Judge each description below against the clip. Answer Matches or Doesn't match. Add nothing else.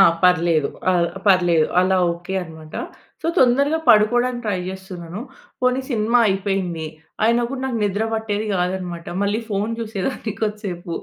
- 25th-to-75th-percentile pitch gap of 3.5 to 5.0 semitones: Matches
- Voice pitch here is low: Doesn't match